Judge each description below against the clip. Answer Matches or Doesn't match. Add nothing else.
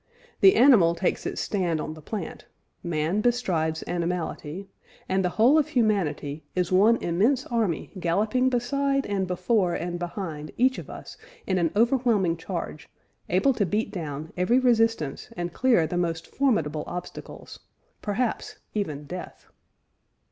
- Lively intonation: Matches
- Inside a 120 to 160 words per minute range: Matches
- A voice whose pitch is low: Doesn't match